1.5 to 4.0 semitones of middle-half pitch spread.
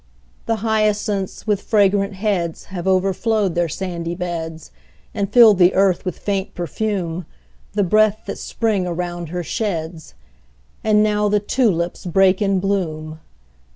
Yes: average, 3.2 semitones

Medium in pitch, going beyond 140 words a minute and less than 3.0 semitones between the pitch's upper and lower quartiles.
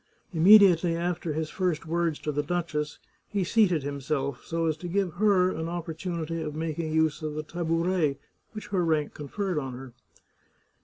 Yes: medium, 165 Hz; average, 165 wpm; narrow, 2.6 semitones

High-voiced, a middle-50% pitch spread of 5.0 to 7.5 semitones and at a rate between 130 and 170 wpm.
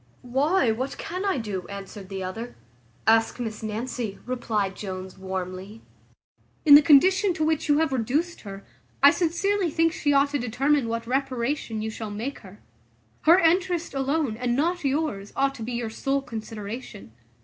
Yes: very high, 250 Hz; wide, 5.5 semitones; average, 165 wpm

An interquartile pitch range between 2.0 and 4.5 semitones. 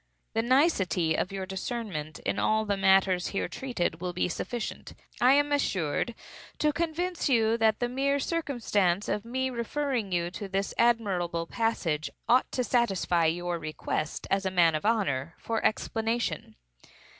No: wide, 5.6 semitones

